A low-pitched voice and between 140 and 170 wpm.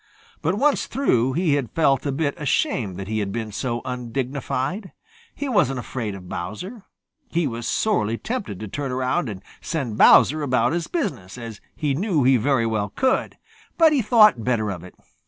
No: low, 130 Hz; average, 180 wpm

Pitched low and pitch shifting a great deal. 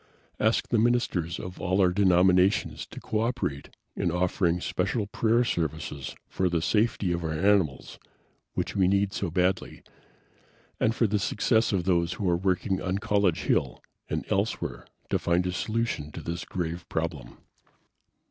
No: very low, 90 Hz; average, 3.2 semitones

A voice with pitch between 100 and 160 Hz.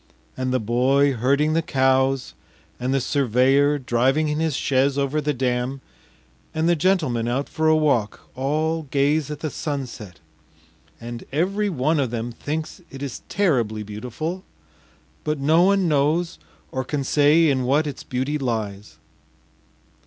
Yes: medium, 140 Hz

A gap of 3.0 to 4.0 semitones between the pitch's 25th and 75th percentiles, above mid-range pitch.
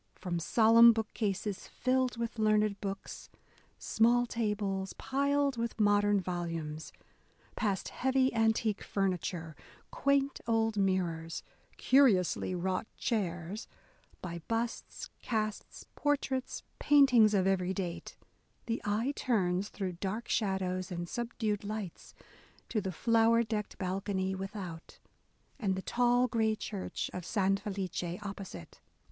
Yes: average, 3.6 semitones; high, 205 Hz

